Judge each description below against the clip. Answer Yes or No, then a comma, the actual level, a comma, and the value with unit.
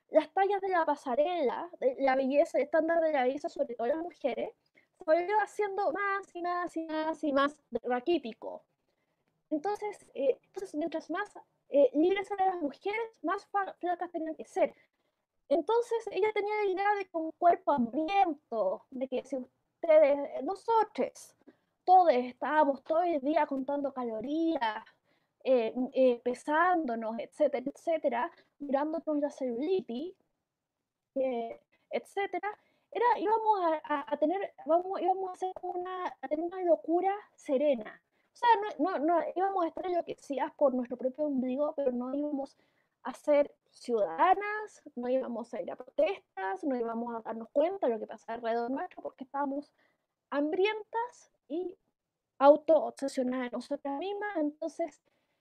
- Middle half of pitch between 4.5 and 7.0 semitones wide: Yes, average, 5.0 semitones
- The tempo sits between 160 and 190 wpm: No, average, 135 wpm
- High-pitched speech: Yes, very high, 310 Hz